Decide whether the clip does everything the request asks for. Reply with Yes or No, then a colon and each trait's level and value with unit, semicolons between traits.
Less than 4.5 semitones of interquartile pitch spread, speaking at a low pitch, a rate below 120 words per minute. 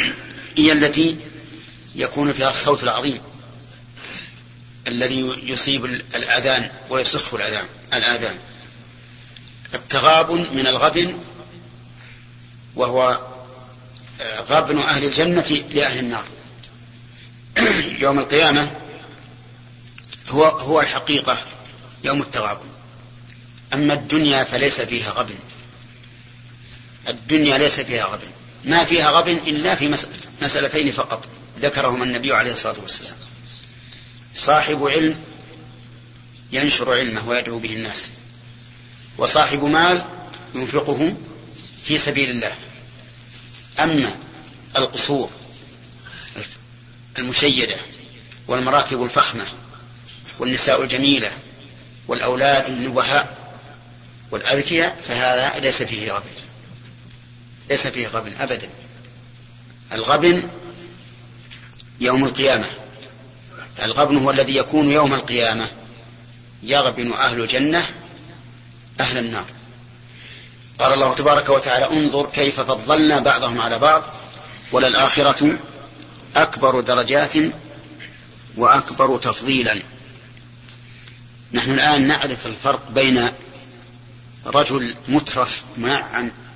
Yes: narrow, 2.6 semitones; low, 125 Hz; average, 80 wpm